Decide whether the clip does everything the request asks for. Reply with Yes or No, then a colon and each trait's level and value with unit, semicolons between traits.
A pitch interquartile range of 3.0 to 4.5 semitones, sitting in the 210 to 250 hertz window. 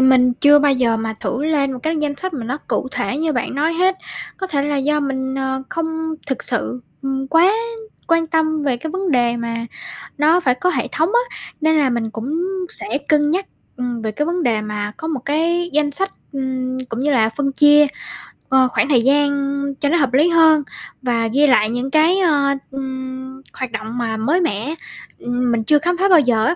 No: average, 4.2 semitones; very high, 280 Hz